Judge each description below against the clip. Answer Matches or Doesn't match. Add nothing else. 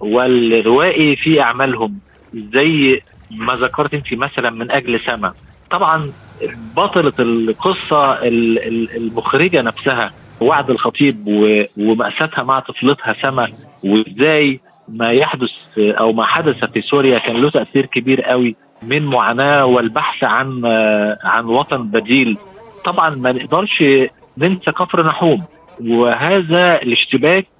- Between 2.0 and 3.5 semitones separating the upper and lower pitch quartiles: Doesn't match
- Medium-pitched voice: Doesn't match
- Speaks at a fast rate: Doesn't match